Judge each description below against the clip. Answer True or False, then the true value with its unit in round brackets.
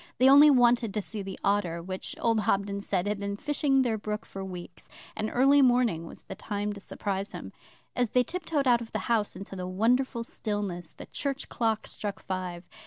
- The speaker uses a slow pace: False (200 wpm)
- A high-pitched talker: True (210 Hz)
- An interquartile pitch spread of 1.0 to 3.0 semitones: False (4.0 semitones)